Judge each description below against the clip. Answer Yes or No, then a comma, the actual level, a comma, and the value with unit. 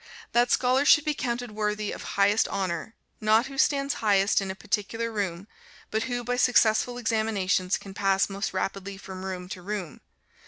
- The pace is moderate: Yes, average, 170 wpm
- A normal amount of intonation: Yes, average, 3.7 semitones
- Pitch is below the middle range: No, high, 210 Hz